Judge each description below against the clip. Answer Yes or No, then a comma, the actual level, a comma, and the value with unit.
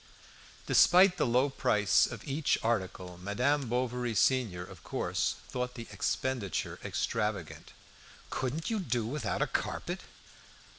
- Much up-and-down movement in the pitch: No, average, 4.4 semitones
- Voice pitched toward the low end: Yes, low, 125 Hz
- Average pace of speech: No, slow, 120 wpm